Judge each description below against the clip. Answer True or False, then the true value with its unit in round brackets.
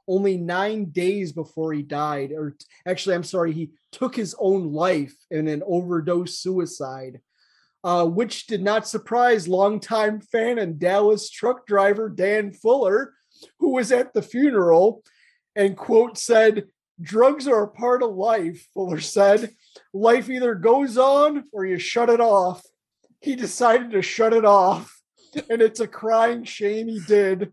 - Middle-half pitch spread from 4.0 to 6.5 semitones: True (4.5 semitones)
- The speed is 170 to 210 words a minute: False (155 wpm)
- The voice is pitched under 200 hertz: False (205 Hz)